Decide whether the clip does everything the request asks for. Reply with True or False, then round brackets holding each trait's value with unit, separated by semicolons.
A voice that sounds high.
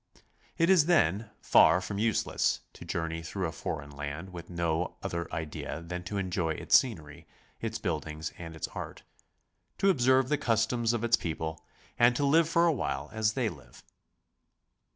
False (95 Hz)